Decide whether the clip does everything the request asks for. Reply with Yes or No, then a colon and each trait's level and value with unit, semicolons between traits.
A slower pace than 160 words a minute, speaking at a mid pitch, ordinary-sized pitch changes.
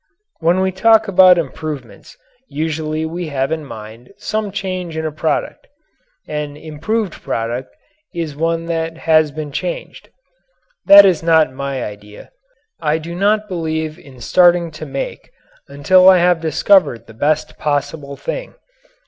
Yes: average, 140 wpm; medium, 160 Hz; average, 3.7 semitones